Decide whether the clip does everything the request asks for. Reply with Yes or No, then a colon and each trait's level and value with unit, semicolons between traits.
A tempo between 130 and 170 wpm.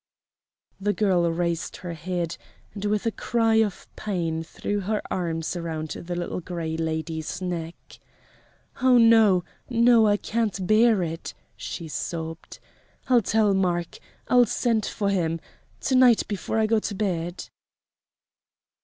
Yes: slow, 135 wpm